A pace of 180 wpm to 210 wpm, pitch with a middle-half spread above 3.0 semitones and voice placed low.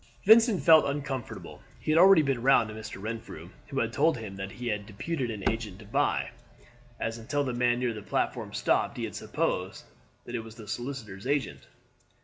Yes: average, 195 wpm; average, 4.6 semitones; low, 120 Hz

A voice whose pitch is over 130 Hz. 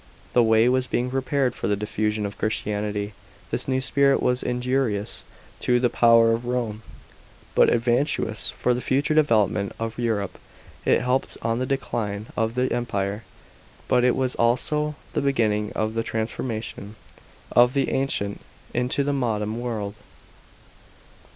No: low, 120 Hz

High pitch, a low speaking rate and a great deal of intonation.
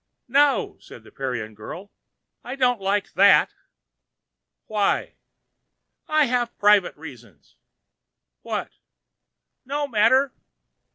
Yes: high, 210 Hz; slow, 95 wpm; wide, 8.4 semitones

